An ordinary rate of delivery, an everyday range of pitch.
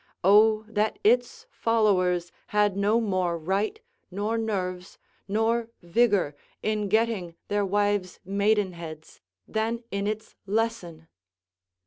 No: slow, 105 wpm; average, 3.2 semitones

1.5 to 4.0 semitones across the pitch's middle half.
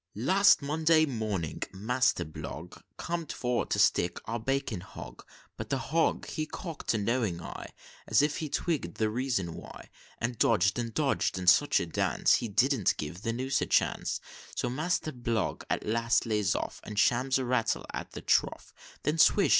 No: average, 5.0 semitones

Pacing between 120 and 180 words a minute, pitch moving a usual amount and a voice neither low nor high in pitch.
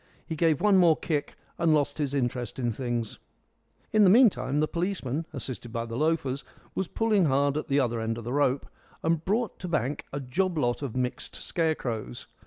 No: average, 195 wpm; average, 5.0 semitones; medium, 145 Hz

